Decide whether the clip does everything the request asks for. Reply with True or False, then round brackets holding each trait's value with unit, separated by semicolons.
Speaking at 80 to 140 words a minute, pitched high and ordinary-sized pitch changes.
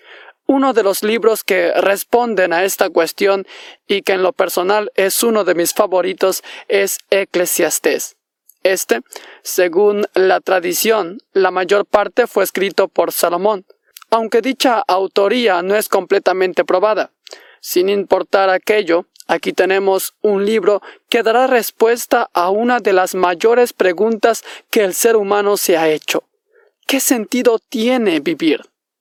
True (135 wpm; 205 Hz; 3.8 semitones)